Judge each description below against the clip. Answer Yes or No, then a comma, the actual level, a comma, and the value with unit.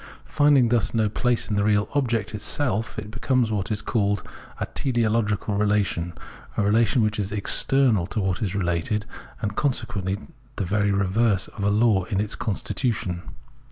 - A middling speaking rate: Yes, average, 170 wpm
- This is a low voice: Yes, low, 105 Hz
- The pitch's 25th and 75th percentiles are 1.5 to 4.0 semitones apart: Yes, narrow, 2.4 semitones